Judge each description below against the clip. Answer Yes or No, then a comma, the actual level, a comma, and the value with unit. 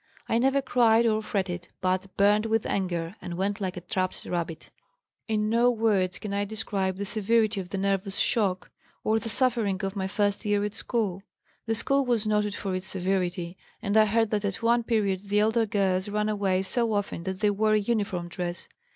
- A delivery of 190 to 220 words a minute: Yes, average, 200 wpm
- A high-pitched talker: Yes, high, 205 Hz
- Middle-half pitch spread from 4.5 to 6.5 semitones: No, narrow, 2.6 semitones